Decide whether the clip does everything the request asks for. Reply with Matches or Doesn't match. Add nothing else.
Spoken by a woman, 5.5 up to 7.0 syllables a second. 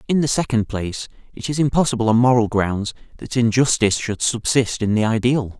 Doesn't match